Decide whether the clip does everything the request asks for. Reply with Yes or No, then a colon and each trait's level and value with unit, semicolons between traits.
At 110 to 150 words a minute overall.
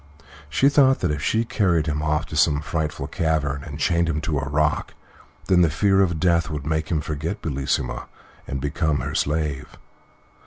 No: average, 185 wpm